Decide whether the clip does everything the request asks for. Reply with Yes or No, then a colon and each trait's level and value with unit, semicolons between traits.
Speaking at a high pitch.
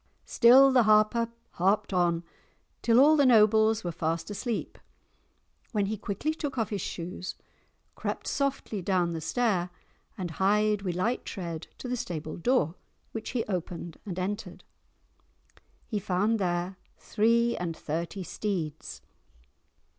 Yes: high, 205 Hz